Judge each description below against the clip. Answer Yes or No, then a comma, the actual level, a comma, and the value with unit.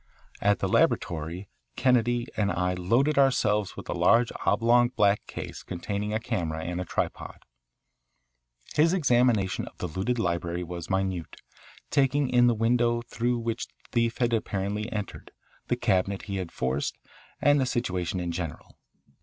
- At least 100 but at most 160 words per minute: Yes, average, 155 wpm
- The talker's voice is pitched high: No, low, 105 Hz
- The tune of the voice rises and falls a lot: No, average, 4.9 semitones